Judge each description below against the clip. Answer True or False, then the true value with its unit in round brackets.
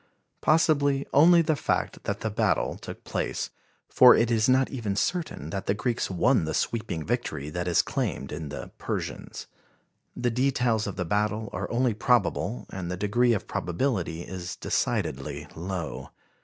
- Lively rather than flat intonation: True (6.1 semitones)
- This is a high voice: False (110 Hz)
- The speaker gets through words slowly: False (160 wpm)